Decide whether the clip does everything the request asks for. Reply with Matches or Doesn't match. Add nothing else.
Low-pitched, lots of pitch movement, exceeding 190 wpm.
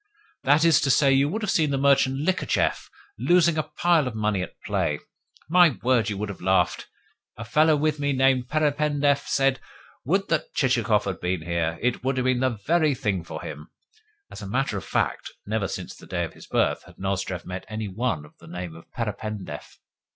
Matches